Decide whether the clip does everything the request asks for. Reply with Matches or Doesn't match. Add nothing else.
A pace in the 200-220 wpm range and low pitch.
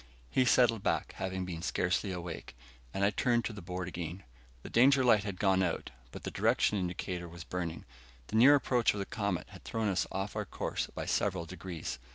Matches